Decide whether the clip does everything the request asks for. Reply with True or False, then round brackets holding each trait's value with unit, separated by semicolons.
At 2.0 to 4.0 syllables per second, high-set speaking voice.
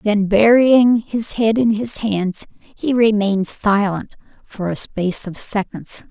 True (3.8 syllables/s; 210 Hz)